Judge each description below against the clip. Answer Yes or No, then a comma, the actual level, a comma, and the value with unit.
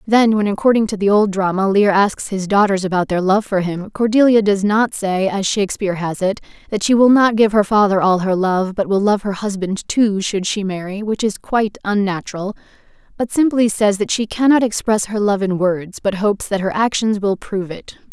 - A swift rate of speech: Yes, fast, 215 wpm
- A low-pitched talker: No, high, 205 Hz